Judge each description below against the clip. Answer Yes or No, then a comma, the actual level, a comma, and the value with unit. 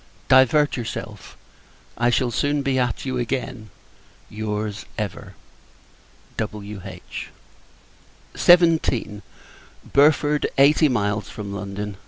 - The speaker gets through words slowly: Yes, slow, 90 wpm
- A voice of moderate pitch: No, low, 120 Hz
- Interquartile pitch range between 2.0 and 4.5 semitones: No, average, 5.0 semitones